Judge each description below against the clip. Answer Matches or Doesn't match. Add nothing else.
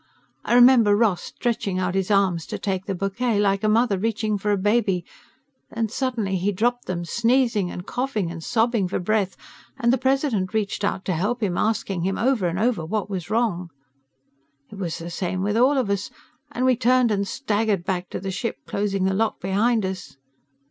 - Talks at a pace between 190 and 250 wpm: Matches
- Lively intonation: Doesn't match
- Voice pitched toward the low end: Doesn't match